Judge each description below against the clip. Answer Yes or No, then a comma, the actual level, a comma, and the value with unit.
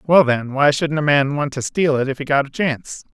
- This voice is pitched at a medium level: Yes, medium, 145 Hz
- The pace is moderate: No, fast, 280 wpm